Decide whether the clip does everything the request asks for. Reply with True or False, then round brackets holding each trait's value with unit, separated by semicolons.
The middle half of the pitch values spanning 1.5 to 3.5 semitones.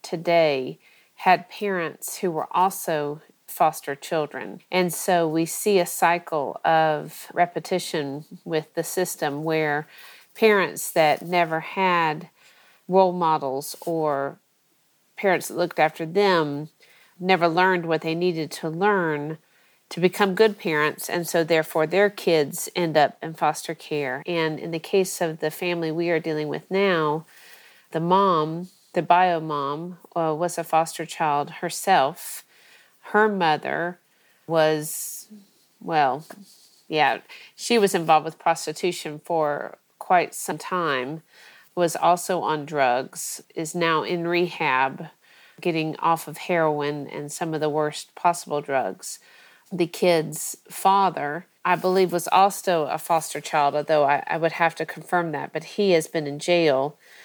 True (2.7 semitones)